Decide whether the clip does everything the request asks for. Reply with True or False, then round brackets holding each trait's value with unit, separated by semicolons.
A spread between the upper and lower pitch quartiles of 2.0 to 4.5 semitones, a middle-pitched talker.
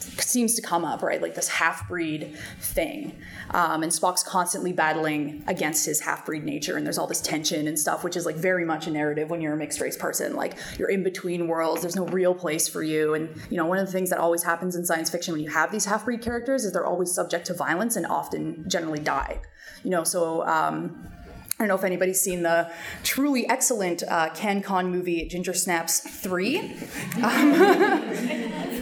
True (2.8 semitones; 175 Hz)